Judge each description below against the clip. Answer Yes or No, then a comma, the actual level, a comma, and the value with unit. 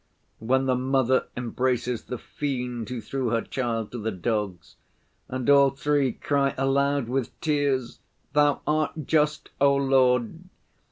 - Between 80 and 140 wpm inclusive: Yes, slow, 135 wpm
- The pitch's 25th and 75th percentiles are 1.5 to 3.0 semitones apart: Yes, narrow, 2.5 semitones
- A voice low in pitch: Yes, low, 130 Hz